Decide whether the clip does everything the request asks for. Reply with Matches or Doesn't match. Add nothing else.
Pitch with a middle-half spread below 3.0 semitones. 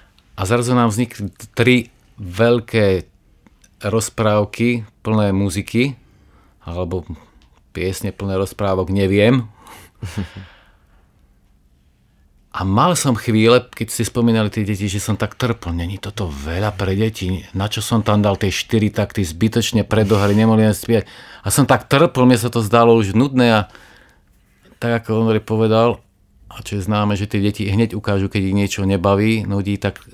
Matches